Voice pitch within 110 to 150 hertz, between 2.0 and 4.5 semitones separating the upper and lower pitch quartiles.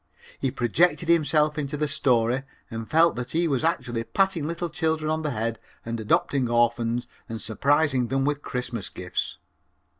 No: low, 135 Hz; average, 5.0 semitones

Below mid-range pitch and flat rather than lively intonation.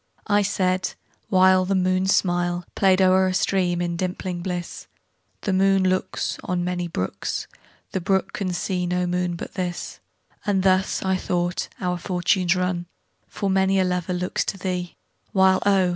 No: medium, 185 Hz; narrow, 1.1 semitones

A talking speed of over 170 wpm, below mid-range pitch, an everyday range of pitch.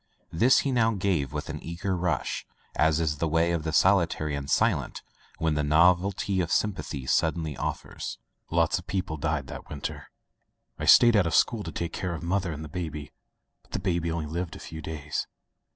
Yes: average, 195 wpm; very low, 85 Hz; average, 3.0 semitones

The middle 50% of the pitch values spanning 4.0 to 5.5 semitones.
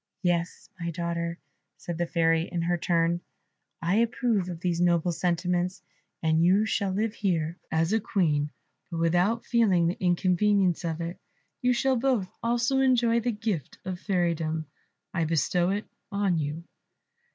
No: average, 3.6 semitones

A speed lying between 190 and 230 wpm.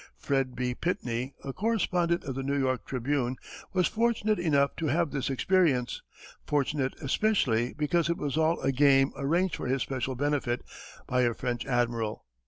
No: average, 165 wpm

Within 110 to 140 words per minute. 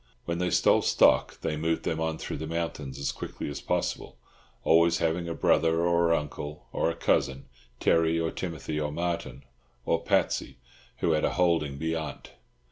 No: average, 160 wpm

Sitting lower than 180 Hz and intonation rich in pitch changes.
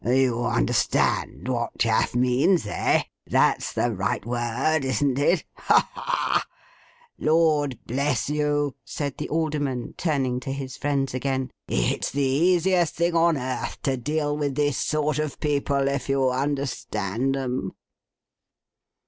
No: medium, 140 Hz; average, 2.9 semitones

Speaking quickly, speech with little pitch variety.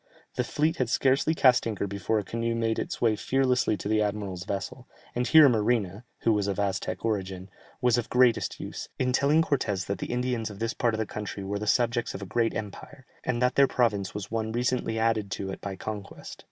No: fast, 220 wpm; average, 3.4 semitones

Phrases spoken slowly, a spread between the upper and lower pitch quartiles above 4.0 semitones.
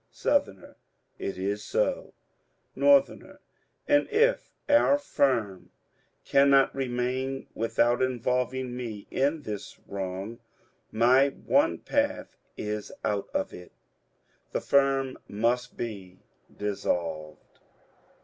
Yes: slow, 100 wpm; average, 4.8 semitones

